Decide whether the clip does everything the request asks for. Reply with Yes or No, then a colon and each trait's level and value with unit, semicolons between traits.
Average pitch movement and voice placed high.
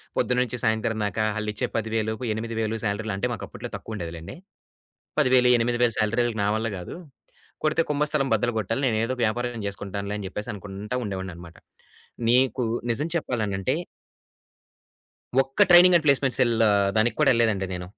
No: average, 3.3 semitones; low, 110 Hz